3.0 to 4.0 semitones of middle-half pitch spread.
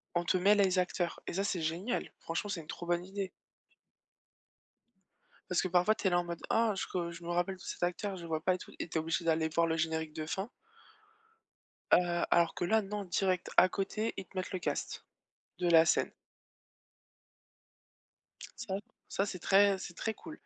No: narrow, 2.4 semitones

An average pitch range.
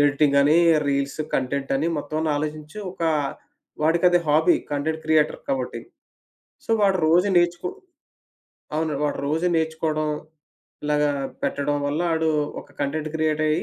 No: narrow, 1.7 semitones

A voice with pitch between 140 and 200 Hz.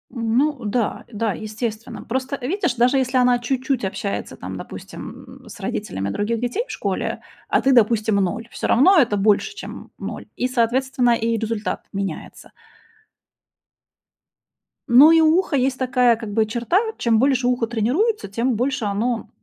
No: high, 240 Hz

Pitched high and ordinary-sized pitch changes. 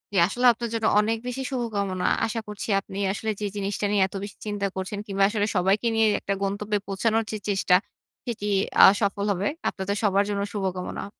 No: high, 205 Hz; narrow, 2.0 semitones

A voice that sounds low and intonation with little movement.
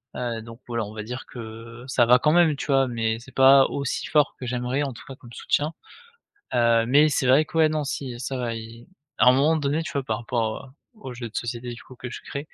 No: low, 125 Hz; average, 3.1 semitones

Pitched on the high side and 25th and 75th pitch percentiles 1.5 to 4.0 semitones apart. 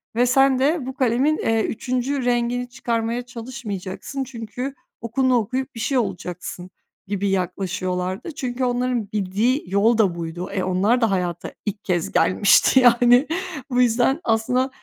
No: high, 235 Hz; average, 4.5 semitones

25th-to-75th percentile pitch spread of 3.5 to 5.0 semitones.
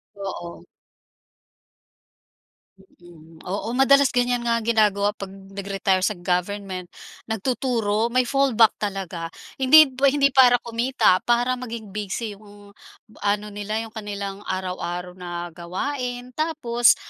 Yes: average, 4.2 semitones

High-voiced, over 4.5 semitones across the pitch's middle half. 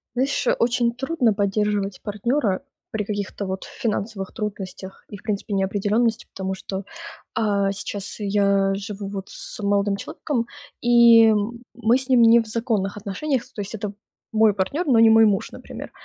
No: high, 210 Hz; average, 2.7 semitones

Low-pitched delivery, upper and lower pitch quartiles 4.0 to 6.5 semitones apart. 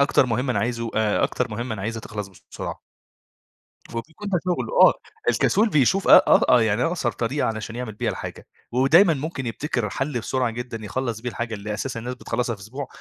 No: low, 120 Hz; average, 3.5 semitones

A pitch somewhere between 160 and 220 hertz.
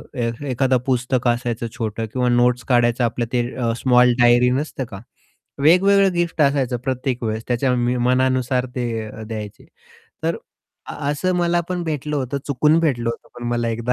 No: low, 125 Hz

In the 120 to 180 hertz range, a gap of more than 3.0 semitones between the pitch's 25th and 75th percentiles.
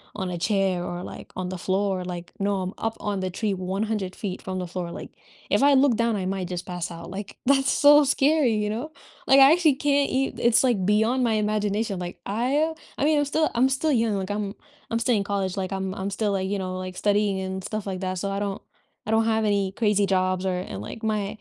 No: high, 205 Hz; average, 3.6 semitones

